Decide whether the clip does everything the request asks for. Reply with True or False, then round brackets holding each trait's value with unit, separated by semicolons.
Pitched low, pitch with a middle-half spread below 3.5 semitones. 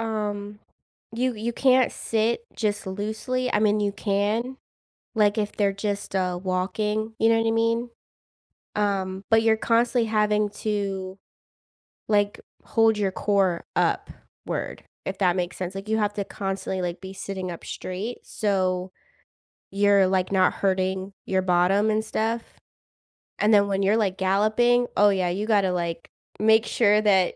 False (205 Hz; 2.4 semitones)